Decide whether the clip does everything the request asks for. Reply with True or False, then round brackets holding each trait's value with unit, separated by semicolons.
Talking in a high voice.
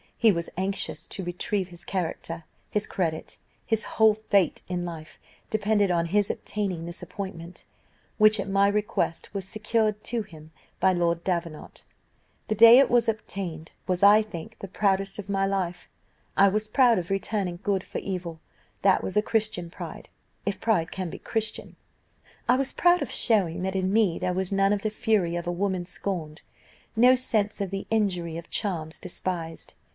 True (195 Hz)